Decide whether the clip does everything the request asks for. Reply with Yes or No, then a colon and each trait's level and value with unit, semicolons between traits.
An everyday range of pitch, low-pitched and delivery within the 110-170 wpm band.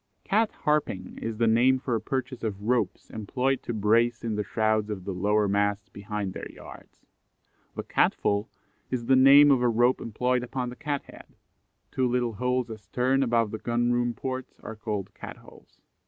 No: average, 3.2 semitones; low, 120 Hz; average, 185 wpm